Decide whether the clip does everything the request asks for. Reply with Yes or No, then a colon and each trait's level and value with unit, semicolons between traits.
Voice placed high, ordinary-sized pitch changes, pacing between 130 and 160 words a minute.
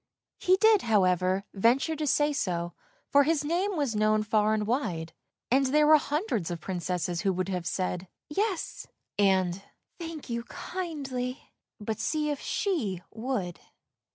No: high, 230 Hz; wide, 8.3 semitones; average, 155 wpm